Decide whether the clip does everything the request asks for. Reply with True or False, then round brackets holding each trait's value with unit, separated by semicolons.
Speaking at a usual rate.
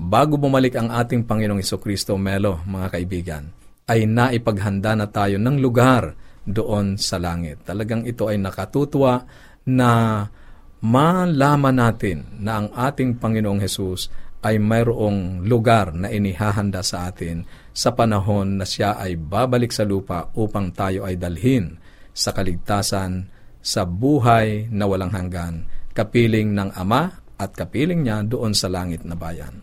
True (135 wpm)